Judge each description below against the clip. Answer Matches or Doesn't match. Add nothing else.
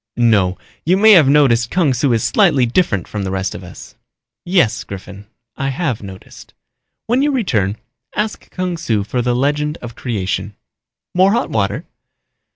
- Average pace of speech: Matches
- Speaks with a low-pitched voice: Matches